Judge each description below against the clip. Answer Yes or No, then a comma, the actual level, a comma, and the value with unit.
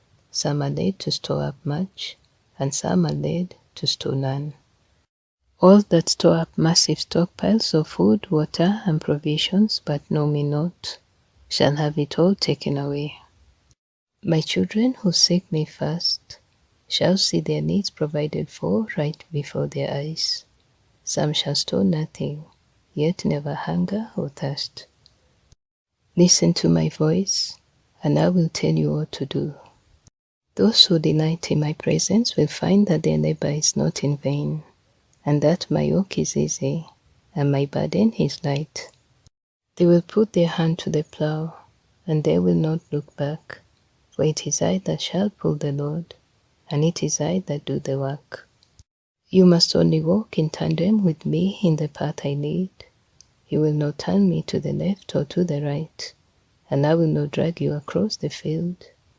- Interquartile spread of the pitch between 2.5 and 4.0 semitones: Yes, average, 3.5 semitones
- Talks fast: No, average, 165 wpm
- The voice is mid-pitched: Yes, medium, 155 Hz